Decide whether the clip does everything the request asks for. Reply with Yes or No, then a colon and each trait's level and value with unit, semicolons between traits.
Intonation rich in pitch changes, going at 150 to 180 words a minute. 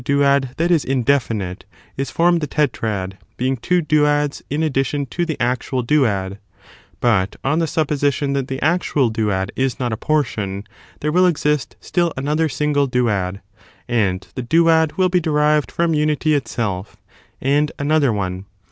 No: average, 4.7 semitones; average, 155 wpm